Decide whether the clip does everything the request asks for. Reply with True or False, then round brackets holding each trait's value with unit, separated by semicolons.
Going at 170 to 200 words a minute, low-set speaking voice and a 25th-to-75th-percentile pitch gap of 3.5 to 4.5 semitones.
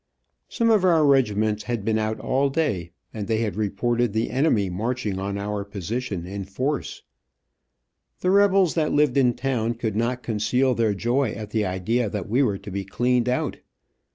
True (175 wpm; 115 Hz; 4.1 semitones)